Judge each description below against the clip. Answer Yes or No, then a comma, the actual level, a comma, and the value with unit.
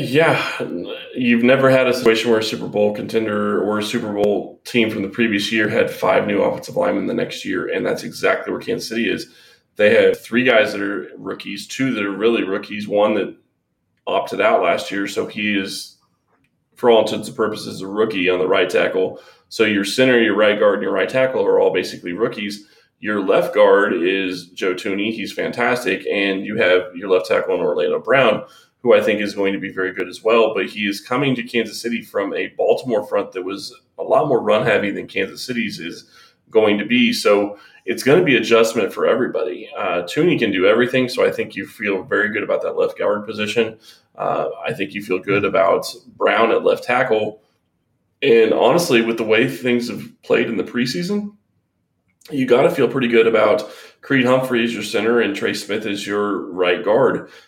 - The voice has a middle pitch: No, low, 115 Hz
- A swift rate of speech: Yes, fast, 210 wpm